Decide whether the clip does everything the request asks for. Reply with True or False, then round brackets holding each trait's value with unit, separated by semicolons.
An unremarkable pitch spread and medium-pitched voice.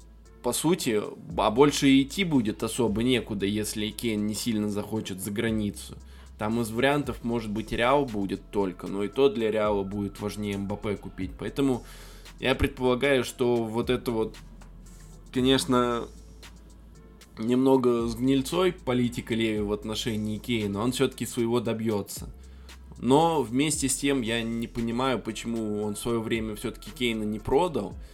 False (3.2 semitones; 115 Hz)